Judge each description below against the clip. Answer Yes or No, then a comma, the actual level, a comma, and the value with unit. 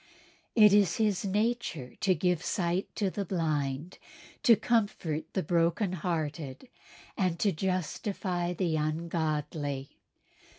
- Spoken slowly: Yes, slow, 115 wpm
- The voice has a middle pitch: Yes, medium, 175 Hz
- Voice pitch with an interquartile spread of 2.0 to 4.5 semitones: Yes, average, 4.1 semitones